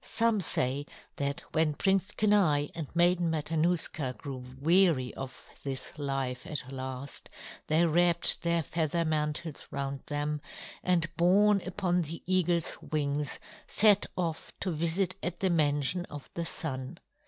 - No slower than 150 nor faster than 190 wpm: No, slow, 135 wpm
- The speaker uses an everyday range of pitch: Yes, average, 3.6 semitones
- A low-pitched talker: No, medium, 160 Hz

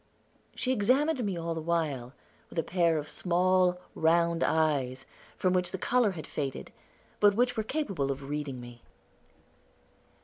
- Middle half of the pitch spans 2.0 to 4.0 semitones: No, average, 5.0 semitones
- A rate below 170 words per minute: Yes, average, 150 wpm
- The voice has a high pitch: No, medium, 170 Hz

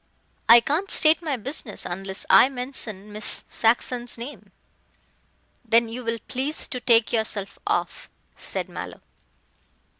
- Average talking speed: No, slow, 125 wpm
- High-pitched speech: Yes, high, 235 Hz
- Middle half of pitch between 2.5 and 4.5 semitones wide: Yes, average, 3.3 semitones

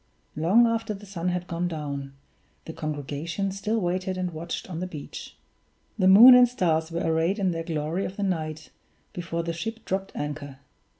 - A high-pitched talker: No, medium, 175 Hz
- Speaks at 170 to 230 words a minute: Yes, average, 180 wpm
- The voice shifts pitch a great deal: No, average, 3.4 semitones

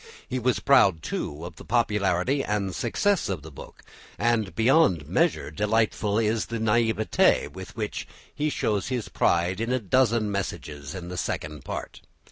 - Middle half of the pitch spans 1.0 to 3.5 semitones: No, average, 4.9 semitones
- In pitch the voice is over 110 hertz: No, low, 105 Hz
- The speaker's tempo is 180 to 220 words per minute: No, average, 160 wpm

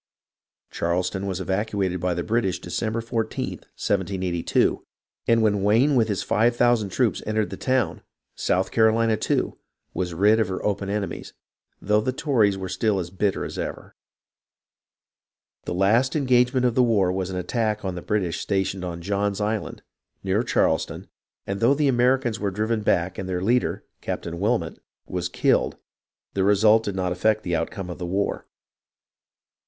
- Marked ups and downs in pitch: No, average, 3.3 semitones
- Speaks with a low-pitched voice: Yes, low, 100 Hz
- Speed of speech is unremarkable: Yes, average, 165 wpm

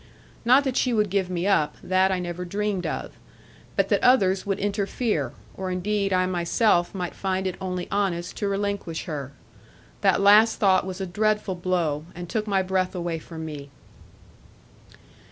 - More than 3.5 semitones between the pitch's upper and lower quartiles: No, narrow, 2.5 semitones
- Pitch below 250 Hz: Yes, high, 190 Hz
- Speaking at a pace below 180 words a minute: Yes, average, 170 wpm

